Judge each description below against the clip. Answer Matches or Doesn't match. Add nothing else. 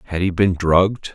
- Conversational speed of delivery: Doesn't match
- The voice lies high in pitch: Doesn't match